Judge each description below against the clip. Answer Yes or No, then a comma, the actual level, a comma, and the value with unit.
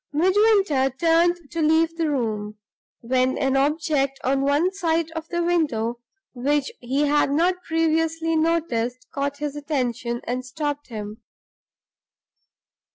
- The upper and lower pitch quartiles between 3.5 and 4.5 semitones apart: Yes, average, 4.1 semitones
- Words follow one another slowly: Yes, slow, 125 wpm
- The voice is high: Yes, very high, 295 Hz